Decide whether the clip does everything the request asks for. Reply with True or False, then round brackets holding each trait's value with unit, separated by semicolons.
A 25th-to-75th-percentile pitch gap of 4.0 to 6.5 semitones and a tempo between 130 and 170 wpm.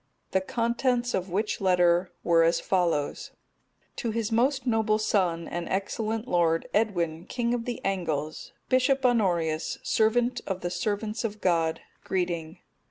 True (5.1 semitones; 140 wpm)